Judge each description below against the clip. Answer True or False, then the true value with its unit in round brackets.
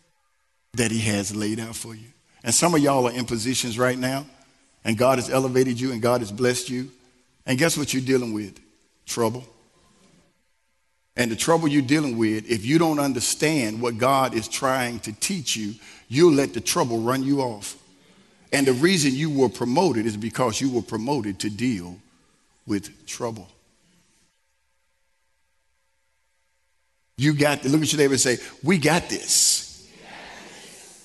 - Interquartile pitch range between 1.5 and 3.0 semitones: False (4.2 semitones)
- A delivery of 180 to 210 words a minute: False (160 wpm)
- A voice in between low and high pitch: False (125 Hz)